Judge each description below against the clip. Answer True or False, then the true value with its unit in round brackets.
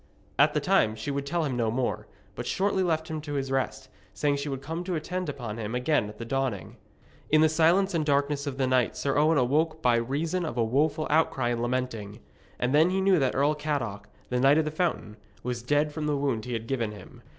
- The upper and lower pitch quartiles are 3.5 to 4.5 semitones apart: True (4.2 semitones)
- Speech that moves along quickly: True (235 wpm)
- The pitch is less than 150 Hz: True (140 Hz)